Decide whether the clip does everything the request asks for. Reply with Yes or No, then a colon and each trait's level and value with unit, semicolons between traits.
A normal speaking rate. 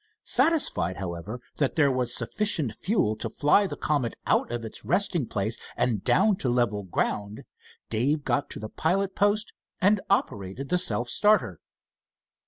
Yes: average, 155 wpm